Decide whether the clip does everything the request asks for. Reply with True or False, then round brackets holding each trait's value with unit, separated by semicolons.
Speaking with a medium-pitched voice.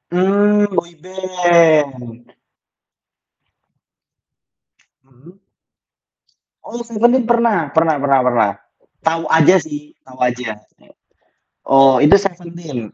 True (160 Hz)